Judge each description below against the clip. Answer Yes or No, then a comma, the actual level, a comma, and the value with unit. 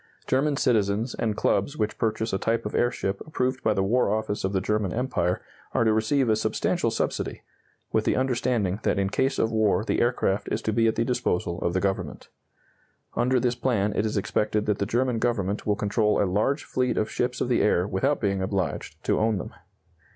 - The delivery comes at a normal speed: No, fast, 210 wpm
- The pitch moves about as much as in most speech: Yes, average, 3.4 semitones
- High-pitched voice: No, low, 110 Hz